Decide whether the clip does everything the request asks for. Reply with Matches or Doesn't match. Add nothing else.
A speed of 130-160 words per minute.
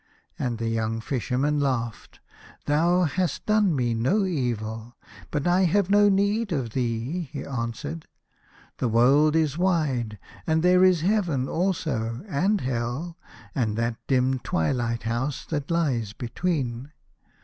Matches